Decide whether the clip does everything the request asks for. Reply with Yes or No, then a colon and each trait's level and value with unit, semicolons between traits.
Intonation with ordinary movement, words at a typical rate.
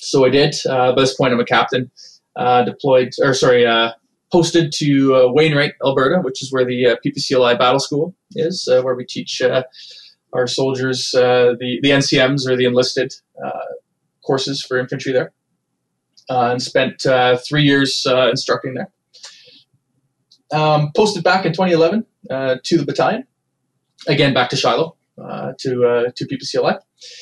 Yes: average, 3.1 semitones; average, 165 wpm